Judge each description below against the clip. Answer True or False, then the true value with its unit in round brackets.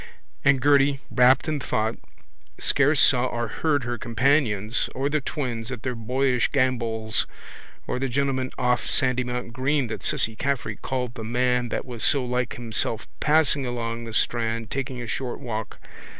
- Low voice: True (125 Hz)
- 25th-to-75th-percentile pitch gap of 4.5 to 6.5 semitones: False (2.8 semitones)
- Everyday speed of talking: True (160 wpm)